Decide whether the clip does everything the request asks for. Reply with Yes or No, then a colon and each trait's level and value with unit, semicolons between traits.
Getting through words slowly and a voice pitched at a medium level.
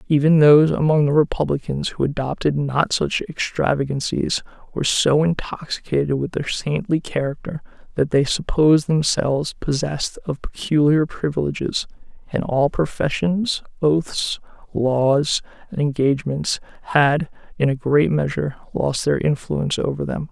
Yes: slow, 125 wpm; medium, 145 Hz